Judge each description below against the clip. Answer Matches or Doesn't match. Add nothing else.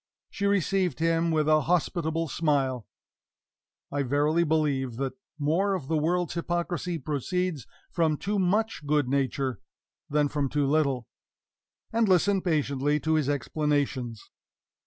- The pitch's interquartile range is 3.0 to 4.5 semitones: Matches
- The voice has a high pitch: Doesn't match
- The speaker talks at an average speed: Doesn't match